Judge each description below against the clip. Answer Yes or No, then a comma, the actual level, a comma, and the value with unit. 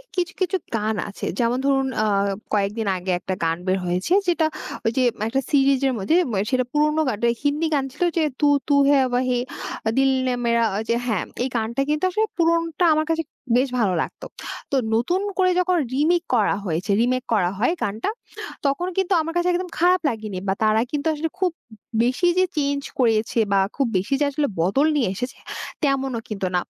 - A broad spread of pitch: Yes, wide, 6.1 semitones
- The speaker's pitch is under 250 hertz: No, very high, 265 Hz